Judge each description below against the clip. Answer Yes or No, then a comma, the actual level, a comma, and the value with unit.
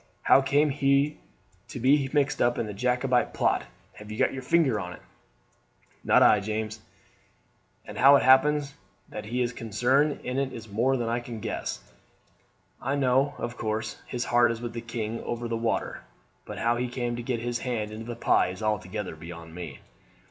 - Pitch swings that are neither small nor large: Yes, average, 3.4 semitones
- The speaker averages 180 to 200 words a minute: Yes, average, 190 wpm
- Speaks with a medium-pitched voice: No, low, 120 Hz